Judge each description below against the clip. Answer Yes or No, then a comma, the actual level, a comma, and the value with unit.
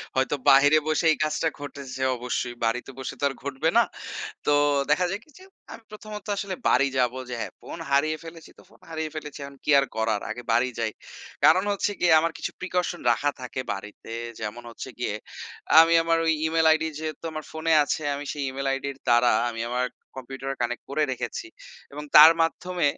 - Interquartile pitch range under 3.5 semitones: No, average, 4.3 semitones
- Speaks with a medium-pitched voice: Yes, medium, 145 Hz